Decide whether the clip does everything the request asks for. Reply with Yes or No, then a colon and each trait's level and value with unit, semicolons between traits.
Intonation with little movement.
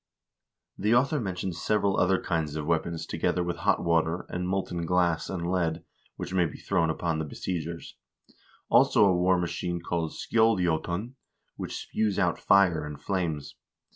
Yes: narrow, 2.3 semitones